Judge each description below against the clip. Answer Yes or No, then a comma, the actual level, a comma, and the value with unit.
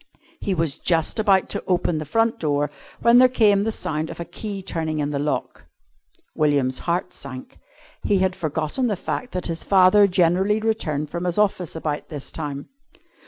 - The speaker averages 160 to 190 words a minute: Yes, average, 180 wpm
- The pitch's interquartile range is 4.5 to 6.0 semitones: Yes, average, 4.9 semitones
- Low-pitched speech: No, medium, 175 Hz